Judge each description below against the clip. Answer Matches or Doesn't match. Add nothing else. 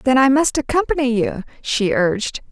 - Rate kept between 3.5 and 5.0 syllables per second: Doesn't match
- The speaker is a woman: Matches